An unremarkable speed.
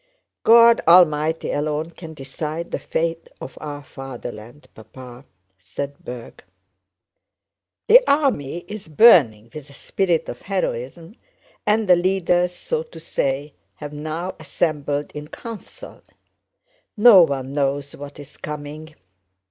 No: slow, 120 wpm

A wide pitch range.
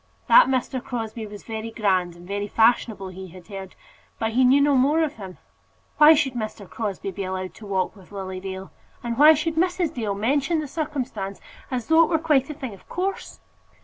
Yes: wide, 6.8 semitones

